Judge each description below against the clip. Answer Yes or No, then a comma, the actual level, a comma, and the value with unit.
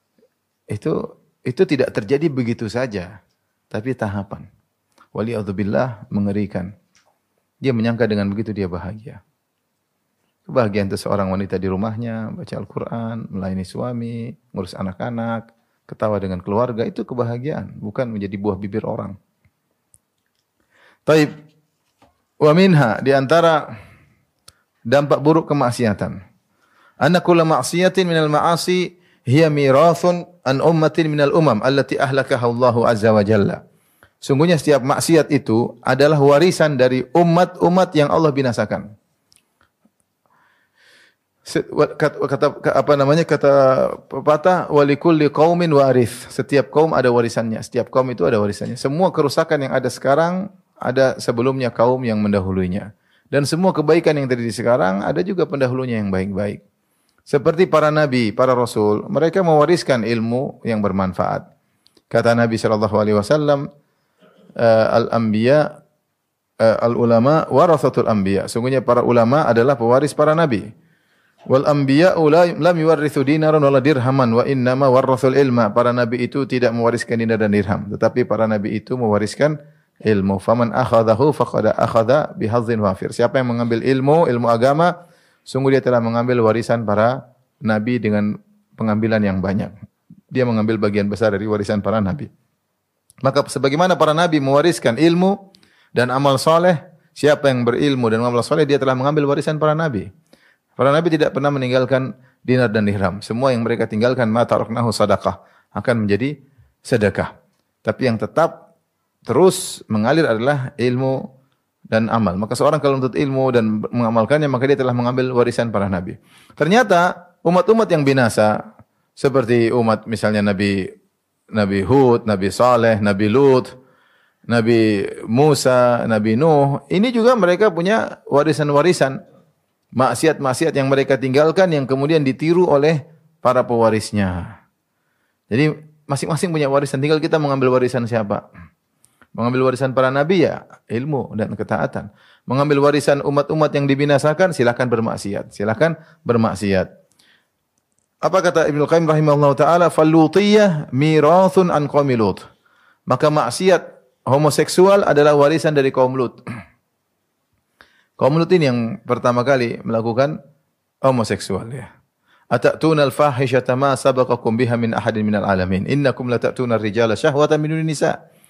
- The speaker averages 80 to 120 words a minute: No, average, 130 wpm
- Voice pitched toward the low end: Yes, low, 130 Hz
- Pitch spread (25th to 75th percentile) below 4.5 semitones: No, average, 5.0 semitones